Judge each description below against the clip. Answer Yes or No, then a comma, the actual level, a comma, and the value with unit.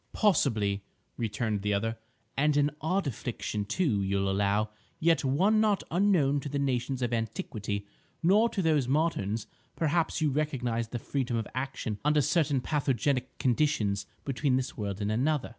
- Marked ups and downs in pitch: Yes, wide, 5.9 semitones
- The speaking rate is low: No, average, 155 wpm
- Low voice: Yes, low, 130 Hz